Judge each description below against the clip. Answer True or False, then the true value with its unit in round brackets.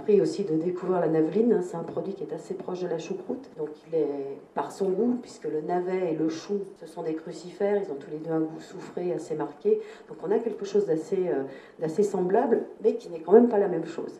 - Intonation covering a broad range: False (4.2 semitones)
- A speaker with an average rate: False (250 wpm)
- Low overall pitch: False (180 Hz)